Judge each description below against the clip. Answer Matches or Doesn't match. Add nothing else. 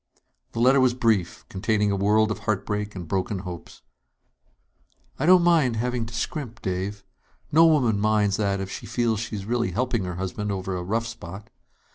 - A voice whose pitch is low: Matches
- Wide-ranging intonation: Doesn't match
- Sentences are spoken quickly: Doesn't match